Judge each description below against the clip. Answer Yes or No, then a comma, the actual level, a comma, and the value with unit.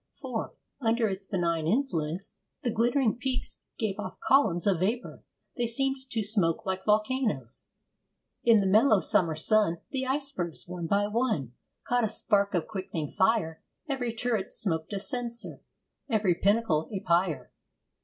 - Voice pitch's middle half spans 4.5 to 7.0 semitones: Yes, average, 5.1 semitones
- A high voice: Yes, high, 210 Hz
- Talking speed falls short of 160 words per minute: Yes, average, 145 wpm